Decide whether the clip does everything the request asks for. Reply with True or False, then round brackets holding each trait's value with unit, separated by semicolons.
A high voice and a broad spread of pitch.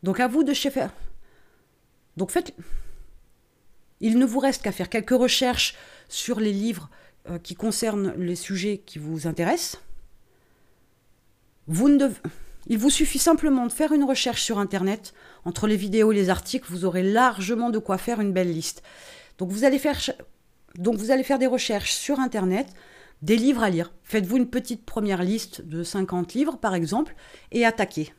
True (215 Hz; 6.1 semitones)